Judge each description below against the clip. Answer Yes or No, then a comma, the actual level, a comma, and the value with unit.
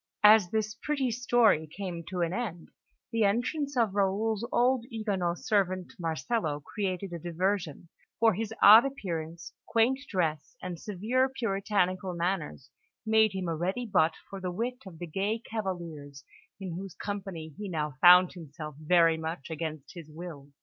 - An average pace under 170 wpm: Yes, average, 155 wpm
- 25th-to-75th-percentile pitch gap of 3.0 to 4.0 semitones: No, average, 4.7 semitones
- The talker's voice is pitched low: No, medium, 185 Hz